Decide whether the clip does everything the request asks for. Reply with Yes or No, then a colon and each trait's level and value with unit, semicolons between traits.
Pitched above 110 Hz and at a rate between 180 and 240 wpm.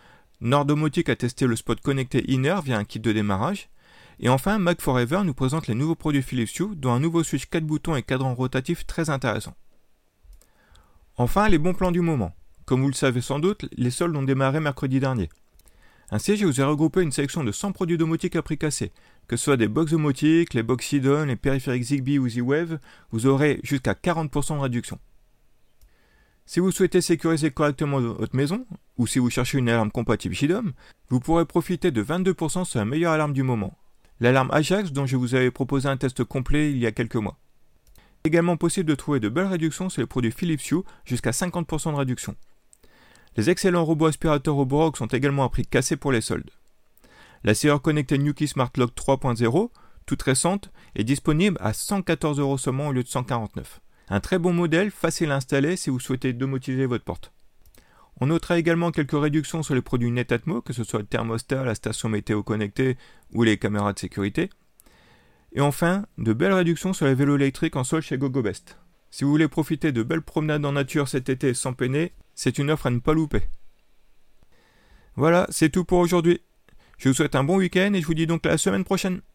Yes: medium, 140 Hz; average, 200 wpm